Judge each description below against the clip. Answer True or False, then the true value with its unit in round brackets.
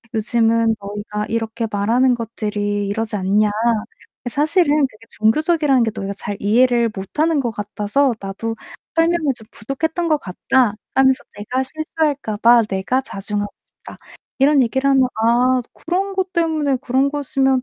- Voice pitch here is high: True (240 Hz)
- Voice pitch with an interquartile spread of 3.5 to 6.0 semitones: True (5.1 semitones)